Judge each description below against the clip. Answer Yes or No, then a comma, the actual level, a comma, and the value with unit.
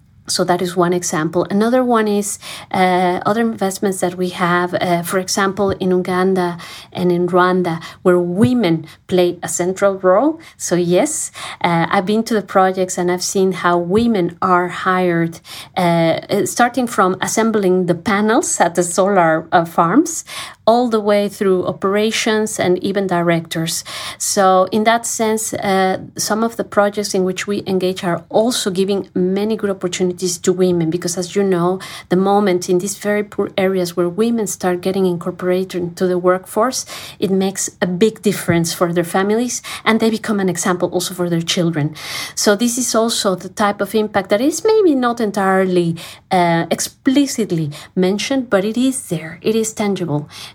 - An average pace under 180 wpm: Yes, average, 170 wpm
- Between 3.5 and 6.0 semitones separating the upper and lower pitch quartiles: No, average, 2.8 semitones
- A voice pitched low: No, high, 190 Hz